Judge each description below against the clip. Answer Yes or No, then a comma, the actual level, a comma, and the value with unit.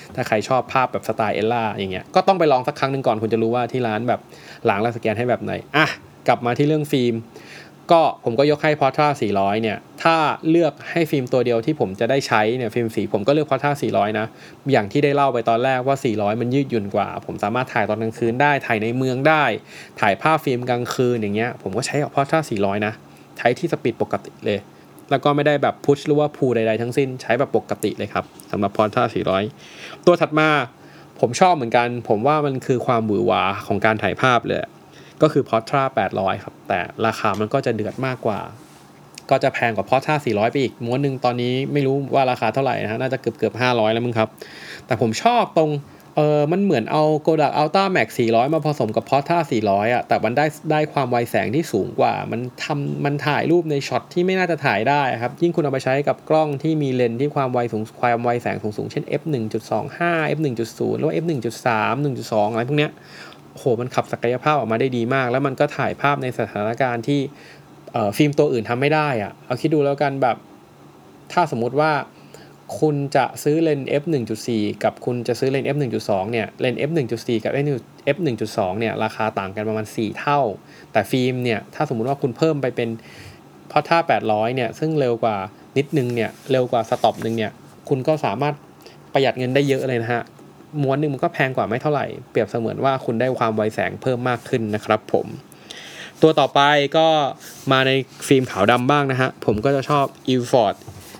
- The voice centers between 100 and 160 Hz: Yes, low, 130 Hz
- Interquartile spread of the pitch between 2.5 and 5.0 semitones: Yes, average, 4.3 semitones